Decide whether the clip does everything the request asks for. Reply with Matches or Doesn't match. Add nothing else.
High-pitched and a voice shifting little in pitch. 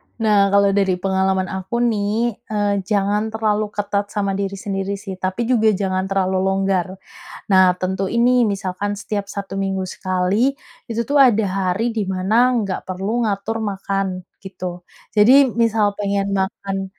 Matches